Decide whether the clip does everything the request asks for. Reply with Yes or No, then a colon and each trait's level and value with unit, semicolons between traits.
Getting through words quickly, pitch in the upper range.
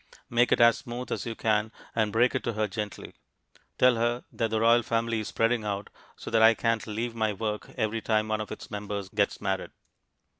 No: fast, 215 wpm; low, 110 Hz